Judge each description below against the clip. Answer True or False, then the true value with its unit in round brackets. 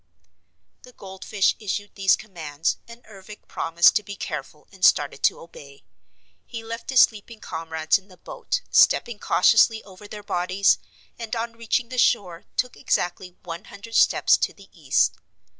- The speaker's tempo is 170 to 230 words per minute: False (160 wpm)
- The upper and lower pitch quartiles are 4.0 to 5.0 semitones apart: True (4.5 semitones)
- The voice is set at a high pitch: True (200 Hz)